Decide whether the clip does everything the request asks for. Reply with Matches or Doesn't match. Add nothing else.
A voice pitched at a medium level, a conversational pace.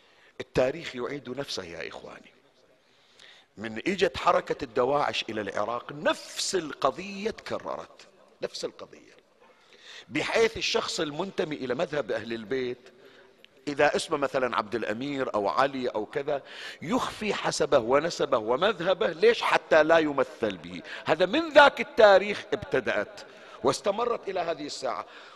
Doesn't match